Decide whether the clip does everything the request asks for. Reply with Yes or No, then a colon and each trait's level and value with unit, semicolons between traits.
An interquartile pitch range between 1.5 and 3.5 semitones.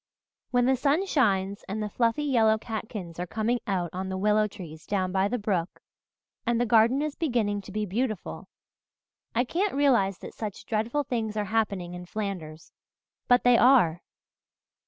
No: average, 4.3 semitones